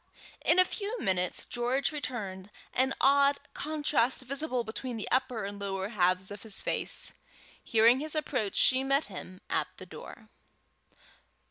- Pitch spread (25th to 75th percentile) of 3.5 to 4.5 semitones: No, wide, 5.6 semitones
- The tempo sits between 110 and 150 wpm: Yes, average, 145 wpm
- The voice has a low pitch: No, high, 245 Hz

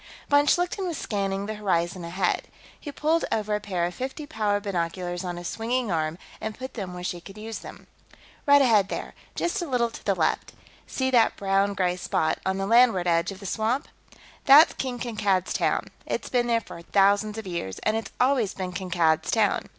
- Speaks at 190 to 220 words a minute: Yes, average, 200 wpm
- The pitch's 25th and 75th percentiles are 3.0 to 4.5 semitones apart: No, average, 5.1 semitones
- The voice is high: Yes, high, 205 Hz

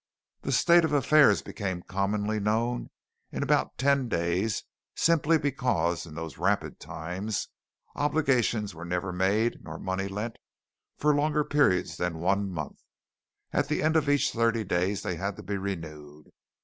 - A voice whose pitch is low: Yes, low, 105 Hz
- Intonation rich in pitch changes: Yes, wide, 7.3 semitones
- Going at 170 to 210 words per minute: No, average, 150 wpm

